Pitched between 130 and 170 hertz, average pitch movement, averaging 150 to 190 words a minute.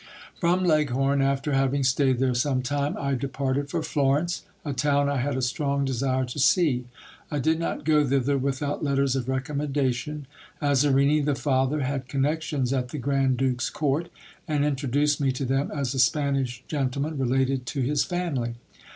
No: medium, 140 Hz; narrow, 1.9 semitones; average, 170 wpm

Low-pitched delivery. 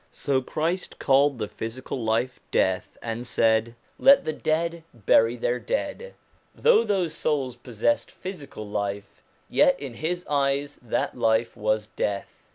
Yes: low, 130 Hz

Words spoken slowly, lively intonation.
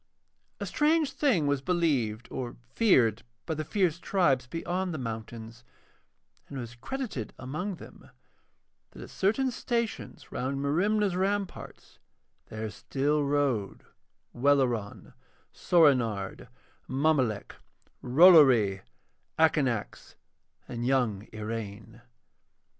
Yes: slow, 100 wpm; wide, 7.2 semitones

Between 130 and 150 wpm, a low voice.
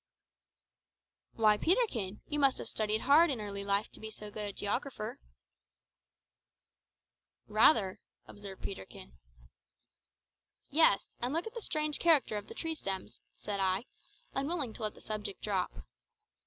No: average, 140 wpm; high, 215 Hz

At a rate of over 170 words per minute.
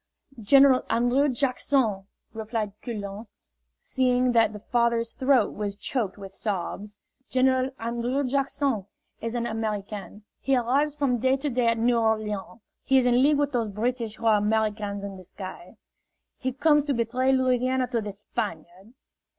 No: average, 165 wpm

